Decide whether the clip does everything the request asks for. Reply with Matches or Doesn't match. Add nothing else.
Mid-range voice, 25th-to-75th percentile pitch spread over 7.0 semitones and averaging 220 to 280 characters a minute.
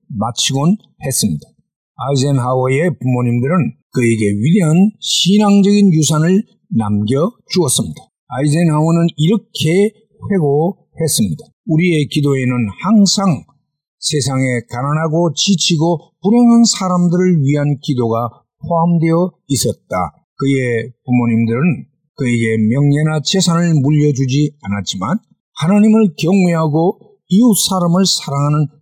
Doesn't match